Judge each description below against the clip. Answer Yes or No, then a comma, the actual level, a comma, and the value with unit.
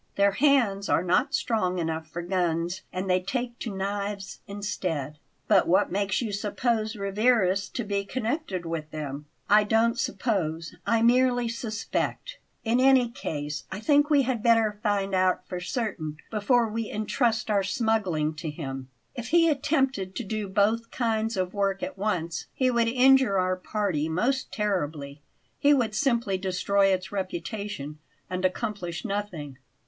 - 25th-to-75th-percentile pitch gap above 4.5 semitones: No, average, 4.1 semitones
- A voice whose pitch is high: Yes, high, 200 Hz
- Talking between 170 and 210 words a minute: No, average, 155 wpm